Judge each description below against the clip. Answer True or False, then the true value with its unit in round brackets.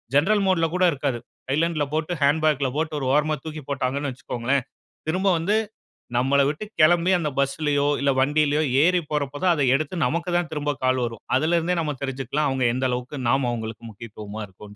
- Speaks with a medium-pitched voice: True (145 Hz)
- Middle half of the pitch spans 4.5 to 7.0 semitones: False (3.4 semitones)